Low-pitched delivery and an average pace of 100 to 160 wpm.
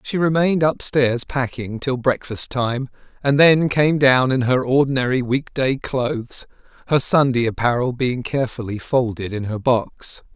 Yes: low, 130 Hz; average, 150 wpm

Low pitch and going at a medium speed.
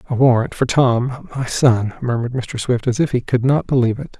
No: low, 125 Hz; fast, 215 wpm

